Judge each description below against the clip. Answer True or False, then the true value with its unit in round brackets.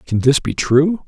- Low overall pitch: False (145 Hz)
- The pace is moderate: False (220 wpm)